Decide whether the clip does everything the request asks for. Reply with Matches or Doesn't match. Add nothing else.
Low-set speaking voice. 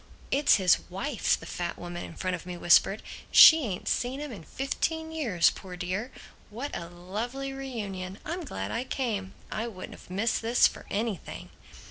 Doesn't match